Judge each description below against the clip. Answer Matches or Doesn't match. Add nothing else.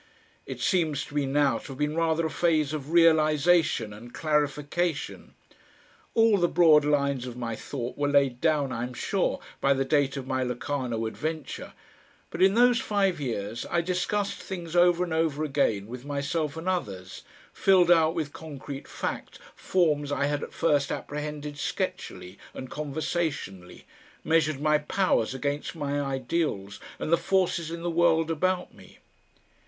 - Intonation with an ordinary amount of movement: Matches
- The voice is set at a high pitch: Doesn't match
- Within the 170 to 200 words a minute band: Doesn't match